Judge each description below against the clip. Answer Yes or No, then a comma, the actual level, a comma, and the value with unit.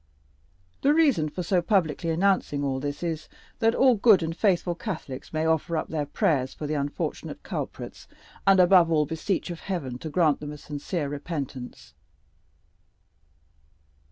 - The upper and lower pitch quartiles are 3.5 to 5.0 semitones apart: Yes, average, 4.0 semitones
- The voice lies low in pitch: No, medium, 160 Hz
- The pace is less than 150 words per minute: No, average, 155 wpm